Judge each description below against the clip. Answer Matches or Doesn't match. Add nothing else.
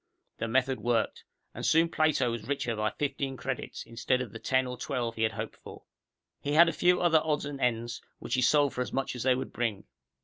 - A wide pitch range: Doesn't match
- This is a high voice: Doesn't match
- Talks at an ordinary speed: Doesn't match